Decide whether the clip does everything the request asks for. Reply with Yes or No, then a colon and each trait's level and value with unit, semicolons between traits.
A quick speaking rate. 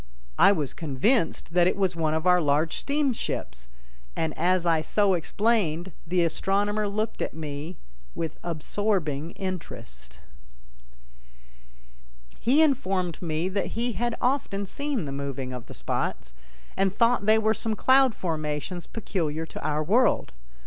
No: average, 140 wpm